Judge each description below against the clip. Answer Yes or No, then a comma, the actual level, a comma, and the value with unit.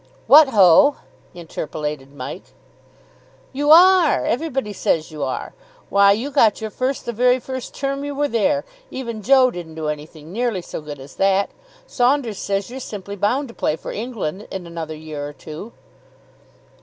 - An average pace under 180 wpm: Yes, average, 165 wpm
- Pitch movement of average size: No, wide, 8.5 semitones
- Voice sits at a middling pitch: No, high, 210 Hz